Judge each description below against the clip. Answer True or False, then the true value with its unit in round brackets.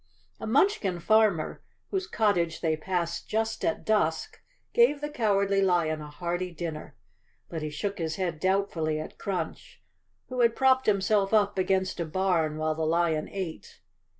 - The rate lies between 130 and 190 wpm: True (155 wpm)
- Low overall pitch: False (185 Hz)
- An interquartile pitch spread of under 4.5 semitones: False (4.8 semitones)